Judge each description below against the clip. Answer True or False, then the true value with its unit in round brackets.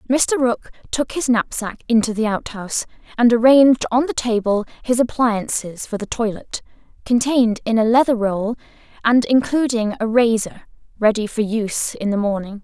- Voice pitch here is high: True (230 Hz)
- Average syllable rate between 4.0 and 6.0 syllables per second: True (5.0 syllables/s)